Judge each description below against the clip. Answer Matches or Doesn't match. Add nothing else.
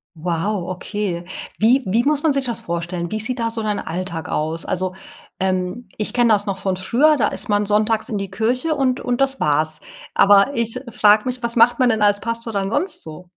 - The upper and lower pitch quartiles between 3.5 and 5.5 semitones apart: Matches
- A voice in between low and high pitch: Doesn't match